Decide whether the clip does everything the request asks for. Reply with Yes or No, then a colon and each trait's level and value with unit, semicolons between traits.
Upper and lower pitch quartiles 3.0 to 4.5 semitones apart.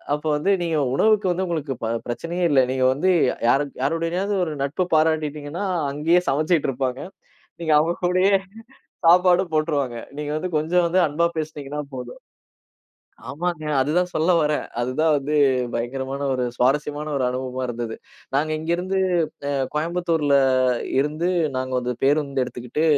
Yes: average, 4.0 semitones